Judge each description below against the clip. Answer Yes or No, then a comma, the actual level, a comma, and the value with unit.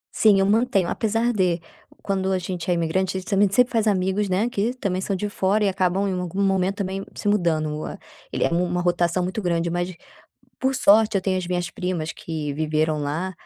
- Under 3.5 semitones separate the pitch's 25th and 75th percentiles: Yes, narrow, 2.6 semitones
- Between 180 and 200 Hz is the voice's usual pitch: Yes, medium, 185 Hz